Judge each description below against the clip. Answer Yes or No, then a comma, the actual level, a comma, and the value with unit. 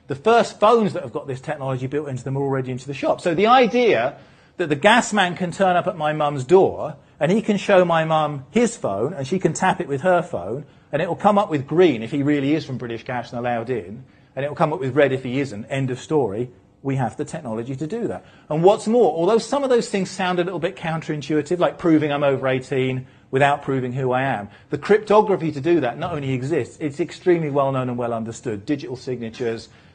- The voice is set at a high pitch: No, medium, 150 Hz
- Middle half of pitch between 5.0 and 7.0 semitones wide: Yes, average, 5.3 semitones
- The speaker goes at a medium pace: No, fast, 245 wpm